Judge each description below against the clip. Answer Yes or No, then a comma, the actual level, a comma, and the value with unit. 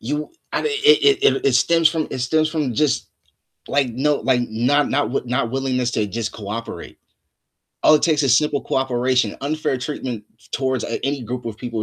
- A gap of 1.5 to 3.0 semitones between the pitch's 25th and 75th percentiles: No, average, 3.8 semitones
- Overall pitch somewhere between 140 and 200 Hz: No, low, 130 Hz